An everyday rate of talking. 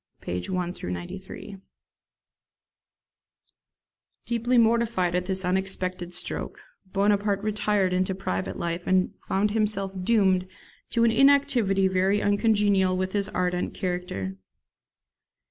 No: slow, 105 wpm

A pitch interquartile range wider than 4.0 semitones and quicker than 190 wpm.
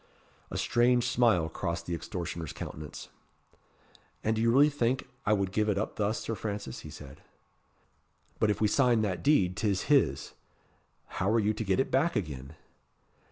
No: average, 5.2 semitones; average, 170 wpm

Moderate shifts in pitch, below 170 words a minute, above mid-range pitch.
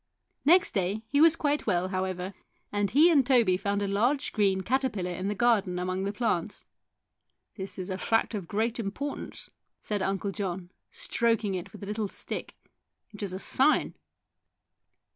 No: average, 4.0 semitones; average, 175 wpm; high, 205 Hz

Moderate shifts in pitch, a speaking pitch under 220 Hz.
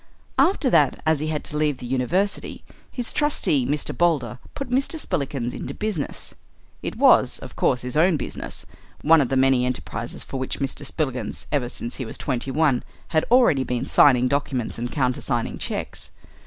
Yes: average, 4.0 semitones; medium, 140 Hz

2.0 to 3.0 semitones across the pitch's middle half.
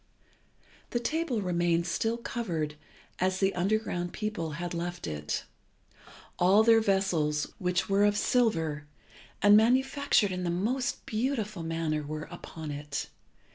No: average, 5.0 semitones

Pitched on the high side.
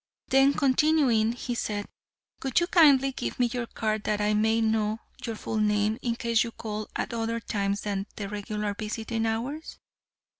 Yes: high, 225 Hz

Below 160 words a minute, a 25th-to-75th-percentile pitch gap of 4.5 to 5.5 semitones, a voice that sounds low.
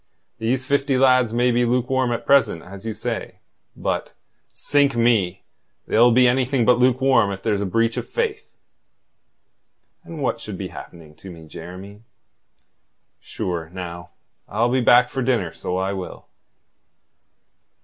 Yes: average, 145 wpm; average, 5.1 semitones; low, 115 Hz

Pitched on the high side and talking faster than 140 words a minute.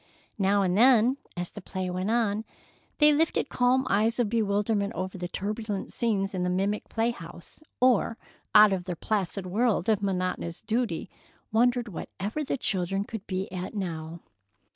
Yes: high, 205 Hz; average, 165 wpm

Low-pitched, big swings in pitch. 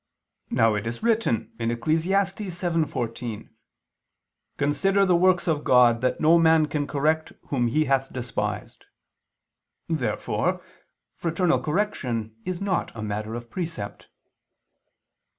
No: medium, 150 Hz; wide, 6.7 semitones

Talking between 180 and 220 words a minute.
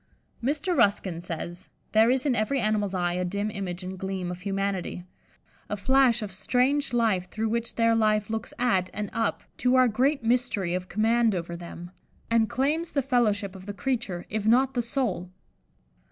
Yes: average, 185 wpm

